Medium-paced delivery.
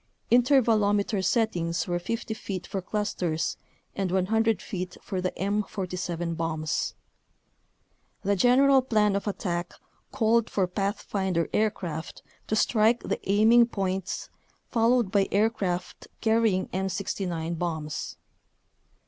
No: slow, 105 wpm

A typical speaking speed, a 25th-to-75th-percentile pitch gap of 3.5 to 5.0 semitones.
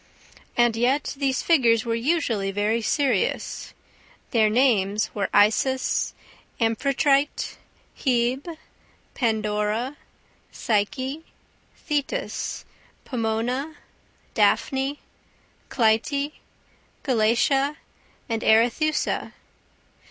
No: slow, 70 wpm; average, 4.1 semitones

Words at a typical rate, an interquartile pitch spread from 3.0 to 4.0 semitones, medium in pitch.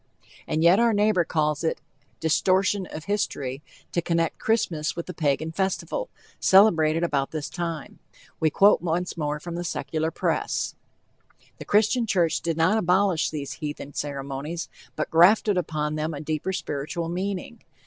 Yes: average, 150 wpm; average, 3.7 semitones; medium, 165 Hz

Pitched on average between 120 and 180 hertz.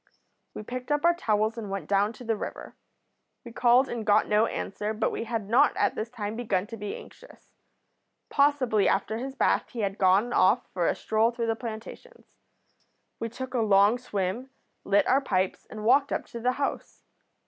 No: high, 225 Hz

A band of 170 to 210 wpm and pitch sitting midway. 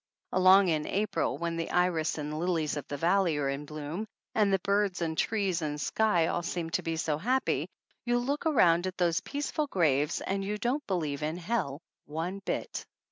Yes: average, 190 wpm; medium, 175 Hz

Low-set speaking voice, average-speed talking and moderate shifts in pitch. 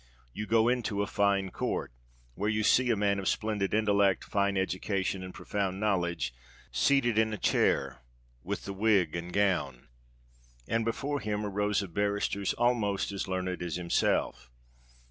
No: low, 100 Hz; average, 160 wpm; narrow, 2.3 semitones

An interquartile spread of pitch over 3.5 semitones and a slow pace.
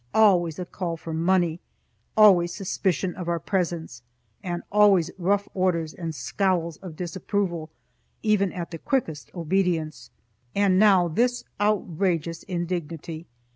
No: average, 2.8 semitones; slow, 125 wpm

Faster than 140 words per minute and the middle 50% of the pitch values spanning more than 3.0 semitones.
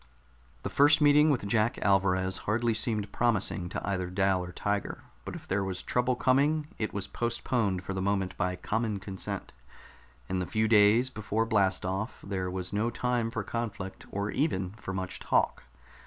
Yes: average, 175 wpm; average, 3.7 semitones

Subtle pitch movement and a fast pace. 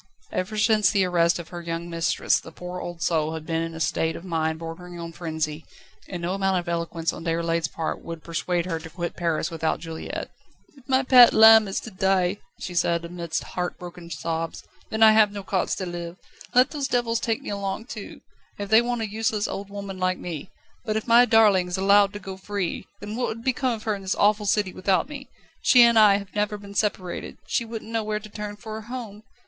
No: average, 4.2 semitones; fast, 225 wpm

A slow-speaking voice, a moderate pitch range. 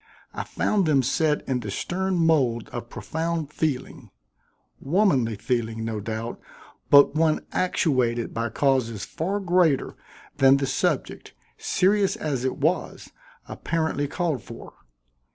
No: slow, 125 wpm; wide, 5.8 semitones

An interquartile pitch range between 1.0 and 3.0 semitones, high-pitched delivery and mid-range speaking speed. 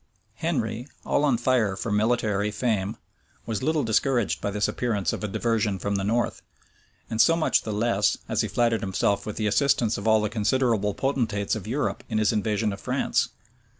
No: average, 2.7 semitones; low, 110 Hz; average, 185 wpm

